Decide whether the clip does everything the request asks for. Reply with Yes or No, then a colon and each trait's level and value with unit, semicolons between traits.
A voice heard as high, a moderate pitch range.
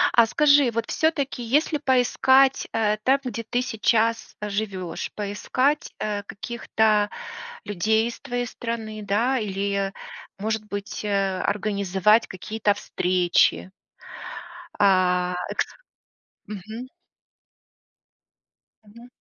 Yes: high, 215 Hz; average, 3.2 semitones